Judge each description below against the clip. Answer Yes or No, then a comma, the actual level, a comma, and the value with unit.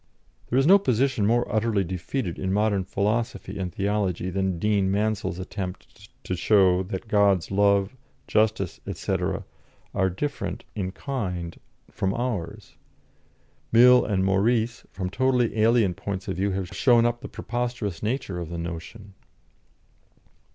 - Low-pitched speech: Yes, low, 100 Hz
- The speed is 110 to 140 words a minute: Yes, slow, 135 wpm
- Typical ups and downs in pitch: Yes, average, 3.6 semitones